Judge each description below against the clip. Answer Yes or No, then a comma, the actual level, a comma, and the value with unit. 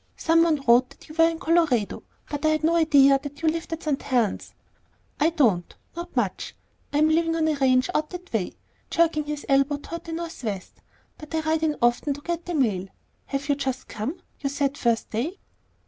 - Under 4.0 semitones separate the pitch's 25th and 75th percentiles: Yes, average, 3.4 semitones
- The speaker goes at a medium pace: No, fast, 210 wpm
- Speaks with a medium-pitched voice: No, very high, 295 Hz